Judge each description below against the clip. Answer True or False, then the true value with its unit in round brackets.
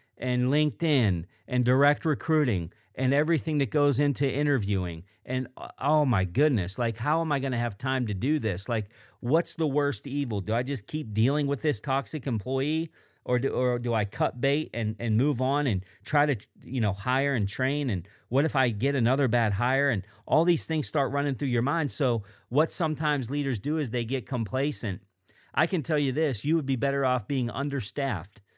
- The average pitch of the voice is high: False (135 Hz)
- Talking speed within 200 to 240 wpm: True (205 wpm)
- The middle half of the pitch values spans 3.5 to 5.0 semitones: True (4.0 semitones)